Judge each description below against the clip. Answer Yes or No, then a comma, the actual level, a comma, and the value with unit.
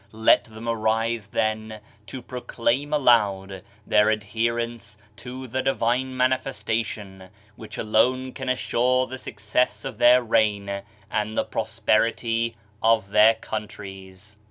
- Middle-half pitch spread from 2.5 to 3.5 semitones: Yes, average, 2.8 semitones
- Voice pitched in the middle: No, low, 115 Hz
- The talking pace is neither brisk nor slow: No, slow, 120 wpm